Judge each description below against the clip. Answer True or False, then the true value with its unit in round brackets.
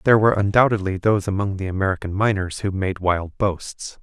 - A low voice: True (100 Hz)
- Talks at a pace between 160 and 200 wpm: True (180 wpm)